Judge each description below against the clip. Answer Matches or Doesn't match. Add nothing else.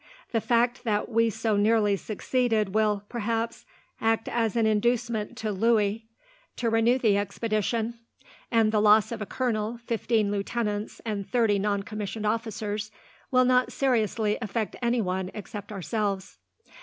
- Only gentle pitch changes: Matches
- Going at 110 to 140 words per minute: Matches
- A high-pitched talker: Matches